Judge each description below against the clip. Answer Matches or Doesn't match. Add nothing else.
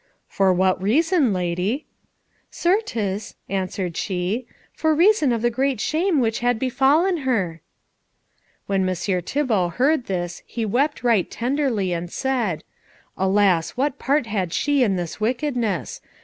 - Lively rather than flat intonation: Matches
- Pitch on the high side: Matches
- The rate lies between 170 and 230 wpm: Doesn't match